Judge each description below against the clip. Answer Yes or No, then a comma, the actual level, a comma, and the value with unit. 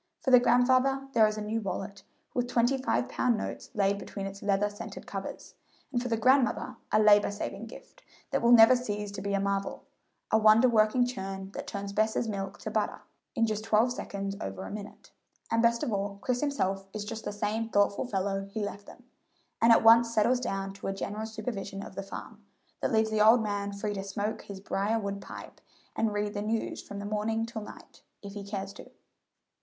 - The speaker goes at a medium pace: No, fast, 210 wpm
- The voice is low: No, high, 210 Hz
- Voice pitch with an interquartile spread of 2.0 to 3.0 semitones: Yes, narrow, 2.4 semitones